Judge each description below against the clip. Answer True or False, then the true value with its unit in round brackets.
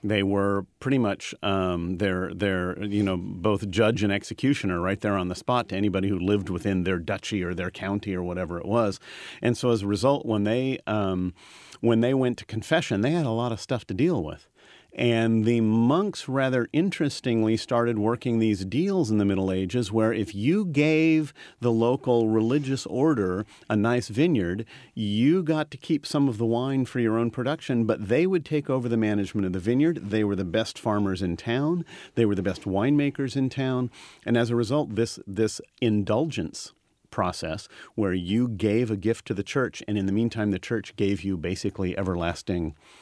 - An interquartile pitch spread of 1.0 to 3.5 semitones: False (4.2 semitones)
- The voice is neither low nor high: False (110 Hz)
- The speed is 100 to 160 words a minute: False (195 wpm)